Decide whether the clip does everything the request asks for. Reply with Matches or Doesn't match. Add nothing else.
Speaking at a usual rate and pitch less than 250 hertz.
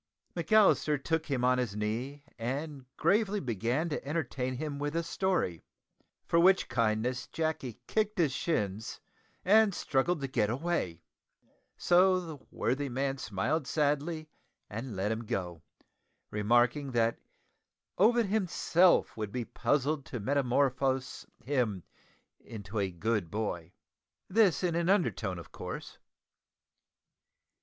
Doesn't match